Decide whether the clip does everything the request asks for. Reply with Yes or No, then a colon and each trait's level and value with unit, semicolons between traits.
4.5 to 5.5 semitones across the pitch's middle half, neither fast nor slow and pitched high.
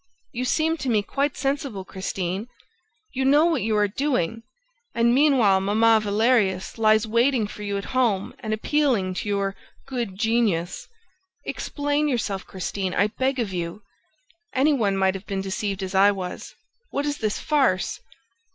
Yes: average, 5.1 semitones; average, 160 wpm; high, 215 Hz